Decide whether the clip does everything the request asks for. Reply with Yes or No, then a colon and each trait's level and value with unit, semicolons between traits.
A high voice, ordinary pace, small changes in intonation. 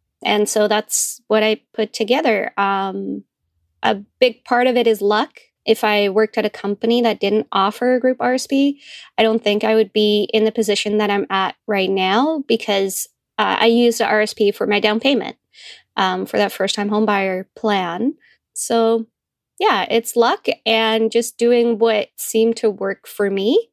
Yes: high, 220 Hz; average, 180 wpm; narrow, 2.2 semitones